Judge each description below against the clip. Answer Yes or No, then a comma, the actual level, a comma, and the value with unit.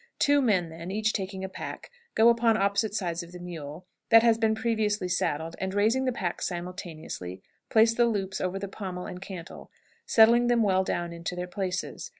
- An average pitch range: Yes, average, 3.8 semitones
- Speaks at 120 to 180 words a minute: No, average, 190 wpm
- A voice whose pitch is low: No, high, 190 Hz